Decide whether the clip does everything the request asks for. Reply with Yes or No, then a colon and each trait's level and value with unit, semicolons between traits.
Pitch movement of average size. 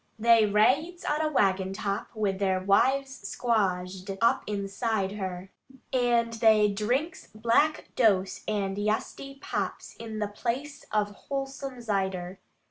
Yes: average, 4.1 semitones